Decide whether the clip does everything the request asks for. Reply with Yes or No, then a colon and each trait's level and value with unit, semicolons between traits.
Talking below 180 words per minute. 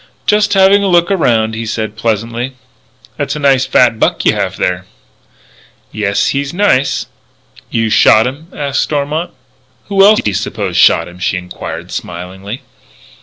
Yes: average, 155 wpm